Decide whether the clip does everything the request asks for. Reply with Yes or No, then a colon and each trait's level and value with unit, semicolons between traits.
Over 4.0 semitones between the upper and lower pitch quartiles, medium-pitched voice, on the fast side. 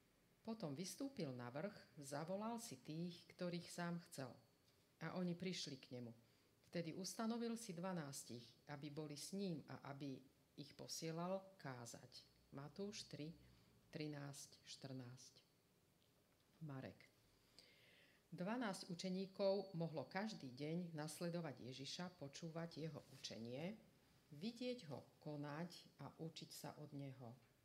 No: average, 4.8 semitones; medium, 155 Hz; slow, 110 wpm